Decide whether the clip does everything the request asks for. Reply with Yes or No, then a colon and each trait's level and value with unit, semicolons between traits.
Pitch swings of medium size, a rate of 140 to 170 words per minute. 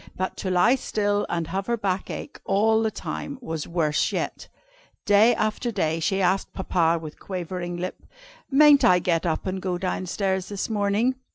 No: average, 3.3 semitones; average, 180 wpm